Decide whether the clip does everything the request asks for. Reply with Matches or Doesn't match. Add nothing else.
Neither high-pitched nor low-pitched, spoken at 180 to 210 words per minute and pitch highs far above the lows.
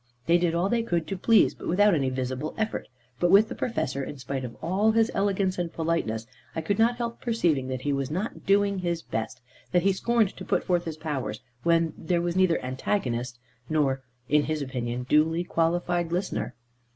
Matches